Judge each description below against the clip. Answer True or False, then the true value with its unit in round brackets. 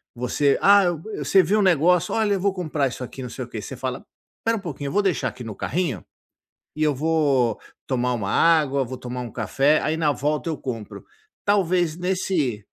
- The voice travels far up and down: True (6.0 semitones)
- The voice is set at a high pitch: False (150 Hz)